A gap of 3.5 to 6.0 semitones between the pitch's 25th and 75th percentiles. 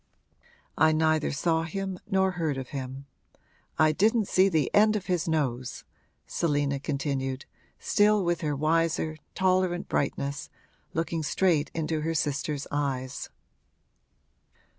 Yes: average, 3.9 semitones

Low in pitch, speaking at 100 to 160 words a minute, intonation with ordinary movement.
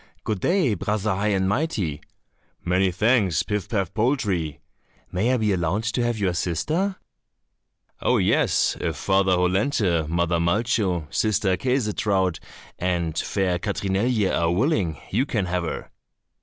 Yes: very low, 95 Hz; slow, 135 wpm; average, 4.0 semitones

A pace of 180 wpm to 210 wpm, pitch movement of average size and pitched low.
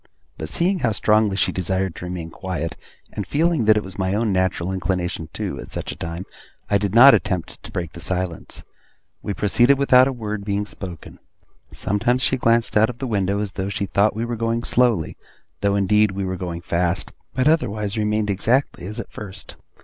Yes: average, 200 wpm; average, 3.7 semitones; low, 100 Hz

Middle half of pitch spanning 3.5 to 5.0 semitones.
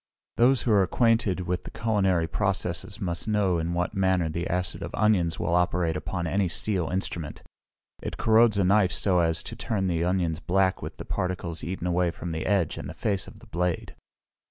No: average, 2.9 semitones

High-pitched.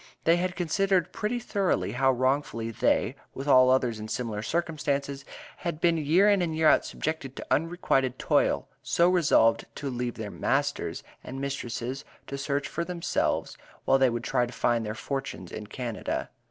No: medium, 140 Hz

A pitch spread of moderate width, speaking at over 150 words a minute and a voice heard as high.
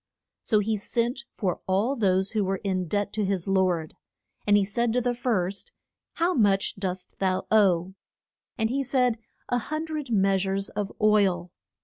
Yes: average, 3.7 semitones; average, 170 wpm; high, 205 Hz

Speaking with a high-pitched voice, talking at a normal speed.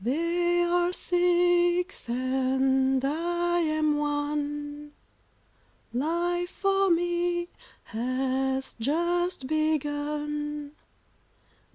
No: very high, 310 Hz; slow, 65 wpm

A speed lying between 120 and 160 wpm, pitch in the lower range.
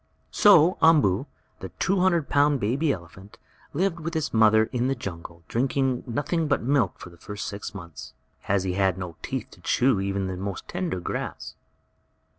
No: average, 175 wpm; low, 115 Hz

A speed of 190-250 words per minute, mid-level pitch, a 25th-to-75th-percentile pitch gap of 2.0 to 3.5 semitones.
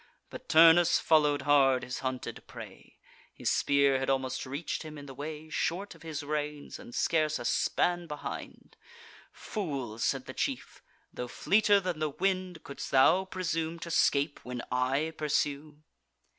No: average, 155 wpm; medium, 150 Hz; average, 3.2 semitones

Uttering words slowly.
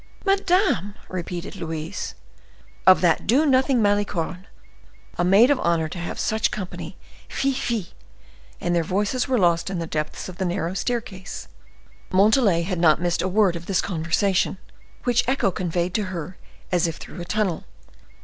No: average, 160 wpm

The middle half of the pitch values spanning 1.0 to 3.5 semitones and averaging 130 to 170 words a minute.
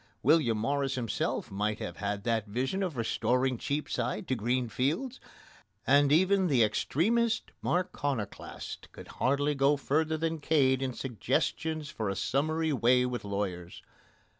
No: wide, 5.4 semitones; average, 140 wpm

